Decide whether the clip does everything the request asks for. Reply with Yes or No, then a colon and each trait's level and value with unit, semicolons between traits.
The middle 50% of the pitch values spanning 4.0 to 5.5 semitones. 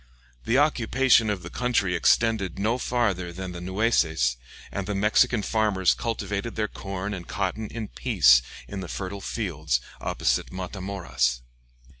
No: average, 3.6 semitones